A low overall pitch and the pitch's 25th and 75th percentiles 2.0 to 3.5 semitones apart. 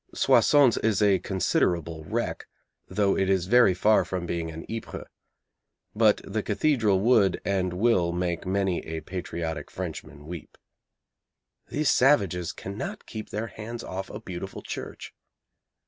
No: very low, 95 Hz; average, 3.9 semitones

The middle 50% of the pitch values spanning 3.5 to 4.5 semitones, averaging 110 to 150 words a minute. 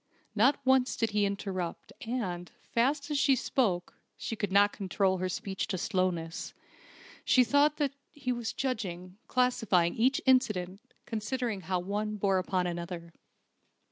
No: wide, 5.4 semitones; average, 140 wpm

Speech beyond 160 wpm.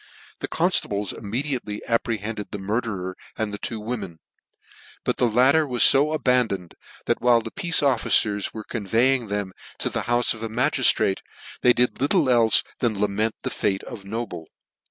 Yes: average, 175 wpm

